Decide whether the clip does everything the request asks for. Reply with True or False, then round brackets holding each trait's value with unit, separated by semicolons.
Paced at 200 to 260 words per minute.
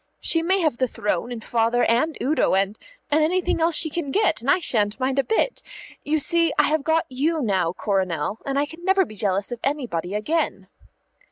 True (205 wpm)